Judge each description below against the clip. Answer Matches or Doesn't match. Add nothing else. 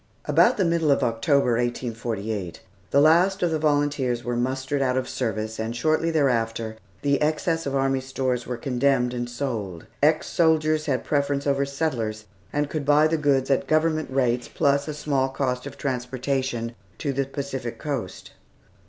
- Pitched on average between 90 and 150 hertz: Matches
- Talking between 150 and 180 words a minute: Matches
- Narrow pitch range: Doesn't match